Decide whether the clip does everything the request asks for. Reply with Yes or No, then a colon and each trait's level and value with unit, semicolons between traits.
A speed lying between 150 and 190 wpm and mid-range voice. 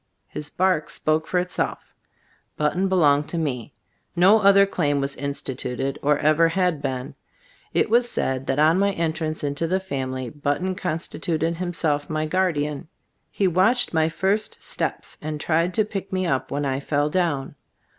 Yes: average, 165 wpm; medium, 160 Hz